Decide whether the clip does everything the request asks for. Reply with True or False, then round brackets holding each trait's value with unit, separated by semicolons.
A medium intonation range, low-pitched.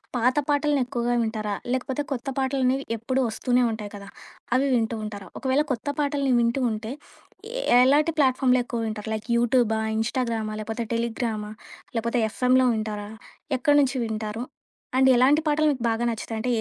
False (3.1 semitones; 240 Hz)